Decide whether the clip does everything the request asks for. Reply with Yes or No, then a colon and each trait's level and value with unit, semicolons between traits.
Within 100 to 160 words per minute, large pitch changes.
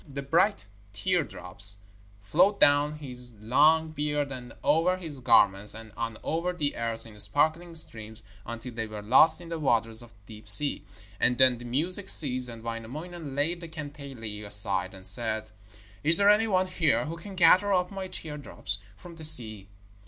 No: average, 175 wpm; wide, 6.6 semitones